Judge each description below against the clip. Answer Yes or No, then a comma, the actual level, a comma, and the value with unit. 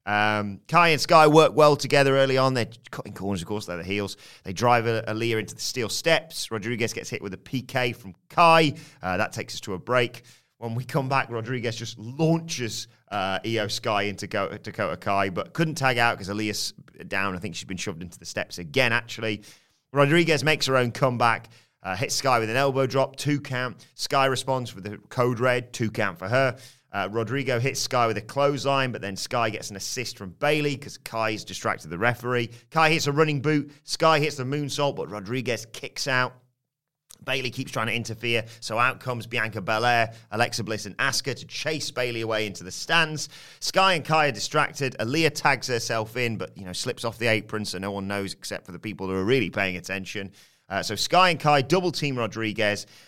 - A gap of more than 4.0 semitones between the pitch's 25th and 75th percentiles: Yes, average, 4.4 semitones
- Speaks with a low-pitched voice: Yes, low, 120 Hz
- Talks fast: Yes, fast, 210 wpm